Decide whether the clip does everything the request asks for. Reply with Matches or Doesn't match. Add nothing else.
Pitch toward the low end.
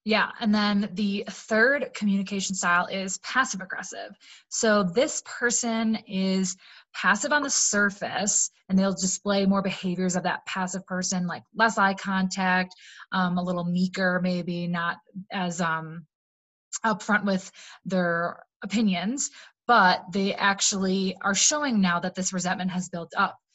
Doesn't match